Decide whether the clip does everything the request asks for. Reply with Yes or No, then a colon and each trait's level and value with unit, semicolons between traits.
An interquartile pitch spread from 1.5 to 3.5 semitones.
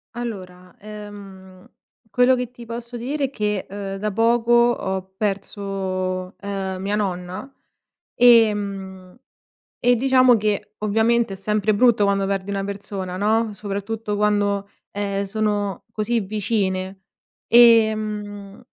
Yes: narrow, 2.5 semitones